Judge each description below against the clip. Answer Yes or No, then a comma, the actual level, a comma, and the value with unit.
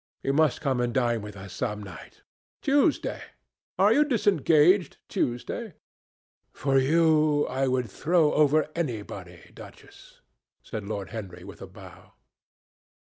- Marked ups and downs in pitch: Yes, wide, 6.5 semitones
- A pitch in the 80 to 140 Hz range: Yes, low, 135 Hz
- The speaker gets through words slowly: Yes, slow, 130 wpm